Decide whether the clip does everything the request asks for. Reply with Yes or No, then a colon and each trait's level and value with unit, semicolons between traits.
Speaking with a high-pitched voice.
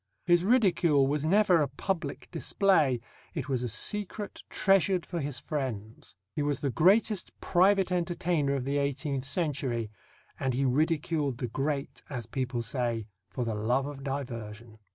No: medium, 140 Hz